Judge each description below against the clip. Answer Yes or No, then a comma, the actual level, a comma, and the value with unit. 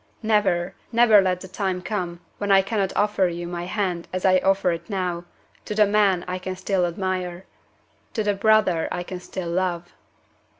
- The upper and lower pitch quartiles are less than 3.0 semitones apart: Yes, narrow, 2.4 semitones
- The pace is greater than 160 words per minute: Yes, average, 180 wpm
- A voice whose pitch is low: No, medium, 185 Hz